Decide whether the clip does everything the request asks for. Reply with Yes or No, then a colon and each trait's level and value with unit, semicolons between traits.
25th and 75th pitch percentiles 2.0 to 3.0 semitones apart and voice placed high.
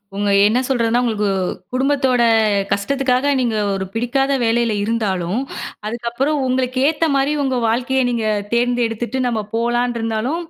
Yes: narrow, 2.6 semitones; high, 240 Hz